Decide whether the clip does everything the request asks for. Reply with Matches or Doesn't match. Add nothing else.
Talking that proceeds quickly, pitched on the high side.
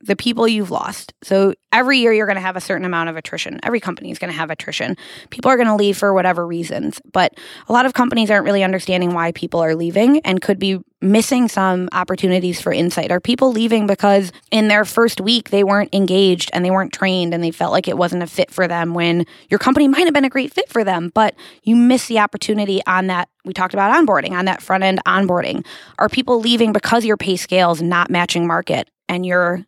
Matches